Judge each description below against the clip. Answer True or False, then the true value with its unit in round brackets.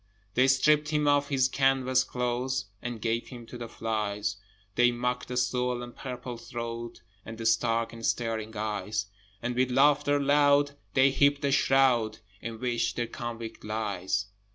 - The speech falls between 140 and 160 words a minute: True (155 wpm)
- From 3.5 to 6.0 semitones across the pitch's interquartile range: False (2.7 semitones)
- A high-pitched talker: False (120 Hz)